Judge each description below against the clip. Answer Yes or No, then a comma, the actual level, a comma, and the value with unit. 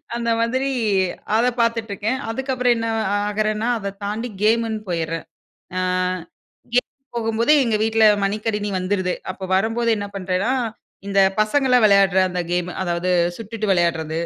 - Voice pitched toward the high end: Yes, high, 215 Hz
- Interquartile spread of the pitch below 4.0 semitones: Yes, average, 3.3 semitones